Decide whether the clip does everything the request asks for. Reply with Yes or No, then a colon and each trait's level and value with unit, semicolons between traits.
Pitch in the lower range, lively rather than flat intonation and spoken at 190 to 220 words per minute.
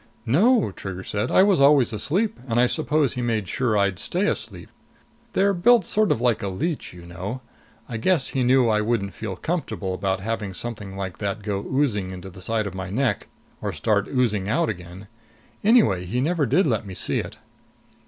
Yes: low, 115 Hz; wide, 6.3 semitones; average, 195 wpm